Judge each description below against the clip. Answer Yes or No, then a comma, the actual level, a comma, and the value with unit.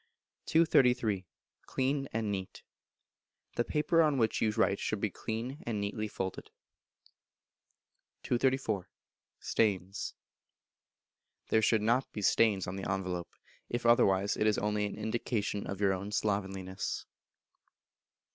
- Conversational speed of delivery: No, slow, 120 wpm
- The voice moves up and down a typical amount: Yes, average, 3.3 semitones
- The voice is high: No, low, 105 Hz